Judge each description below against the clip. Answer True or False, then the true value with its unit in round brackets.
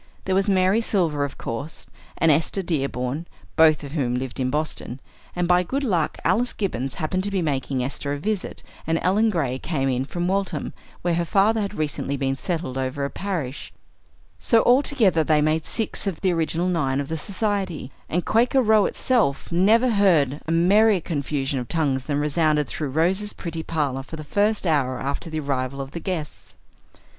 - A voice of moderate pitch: True (160 Hz)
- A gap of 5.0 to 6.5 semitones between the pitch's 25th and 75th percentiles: True (5.5 semitones)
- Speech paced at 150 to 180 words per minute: False (190 wpm)